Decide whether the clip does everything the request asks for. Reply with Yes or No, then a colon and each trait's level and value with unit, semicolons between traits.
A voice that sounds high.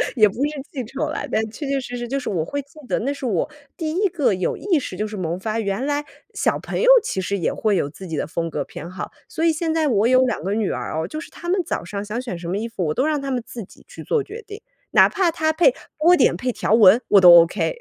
Yes: high, 240 Hz